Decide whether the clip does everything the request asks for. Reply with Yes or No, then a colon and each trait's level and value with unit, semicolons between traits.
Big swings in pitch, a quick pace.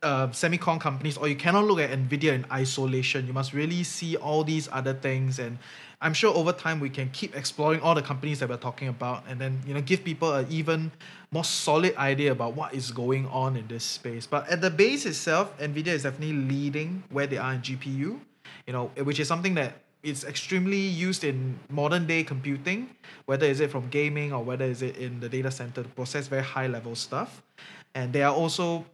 No: average, 3.6 semitones; fast, 215 wpm